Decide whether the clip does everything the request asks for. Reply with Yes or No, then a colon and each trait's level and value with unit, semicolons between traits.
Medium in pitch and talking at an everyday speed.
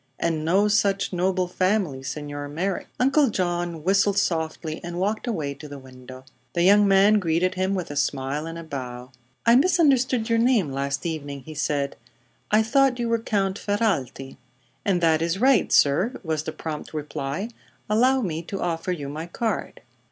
Yes: medium, 175 Hz; average, 175 wpm